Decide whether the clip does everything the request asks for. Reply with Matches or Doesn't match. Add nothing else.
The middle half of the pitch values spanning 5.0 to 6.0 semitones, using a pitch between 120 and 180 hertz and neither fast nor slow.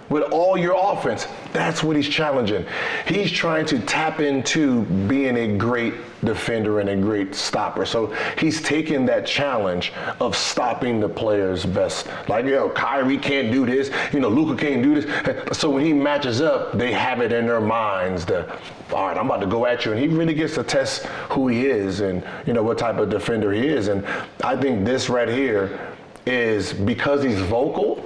Matches